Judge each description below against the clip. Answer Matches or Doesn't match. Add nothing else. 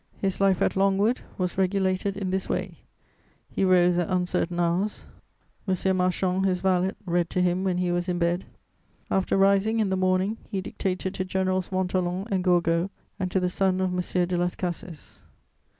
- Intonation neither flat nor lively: Doesn't match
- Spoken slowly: Doesn't match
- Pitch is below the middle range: Doesn't match